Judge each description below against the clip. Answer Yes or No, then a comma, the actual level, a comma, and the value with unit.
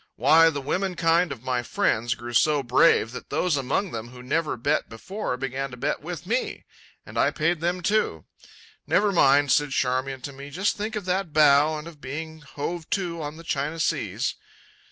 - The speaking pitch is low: No, medium, 150 Hz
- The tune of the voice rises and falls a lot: No, average, 4.3 semitones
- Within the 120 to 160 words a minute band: No, average, 195 wpm